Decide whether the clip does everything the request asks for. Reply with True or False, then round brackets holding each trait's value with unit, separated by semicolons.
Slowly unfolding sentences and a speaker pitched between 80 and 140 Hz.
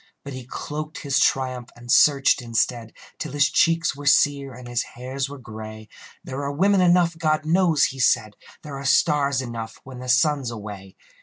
False (180 wpm; 135 Hz)